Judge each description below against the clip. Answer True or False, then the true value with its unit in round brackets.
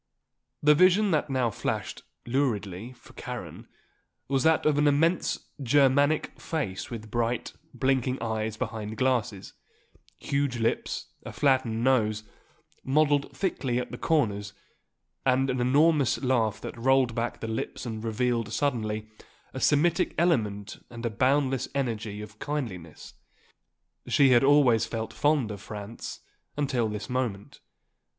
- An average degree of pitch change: True (4.3 semitones)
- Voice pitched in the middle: False (125 Hz)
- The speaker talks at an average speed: False (130 wpm)